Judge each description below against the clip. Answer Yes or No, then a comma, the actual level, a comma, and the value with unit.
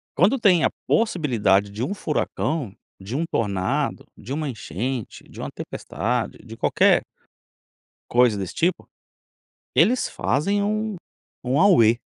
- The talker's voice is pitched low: Yes, low, 130 Hz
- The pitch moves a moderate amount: No, wide, 9.0 semitones